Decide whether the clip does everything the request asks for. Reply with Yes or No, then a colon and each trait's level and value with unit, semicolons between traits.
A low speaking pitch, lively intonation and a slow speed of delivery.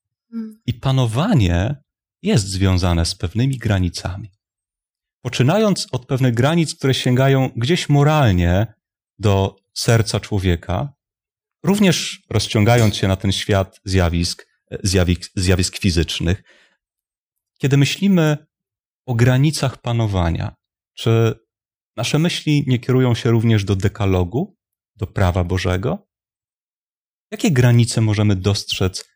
Yes: low, 110 Hz; wide, 5.8 semitones; slow, 100 wpm